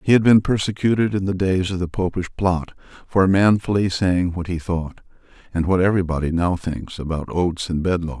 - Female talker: No, male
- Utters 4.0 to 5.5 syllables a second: Yes, 5.4 syllables/s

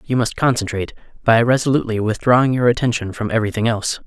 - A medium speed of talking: Yes, average, 160 wpm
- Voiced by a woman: No, male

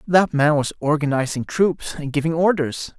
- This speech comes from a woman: No, male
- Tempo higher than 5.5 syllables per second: No, 4.6 syllables/s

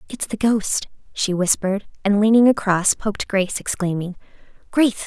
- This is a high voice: Yes, high, 205 Hz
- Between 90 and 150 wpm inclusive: Yes, average, 140 wpm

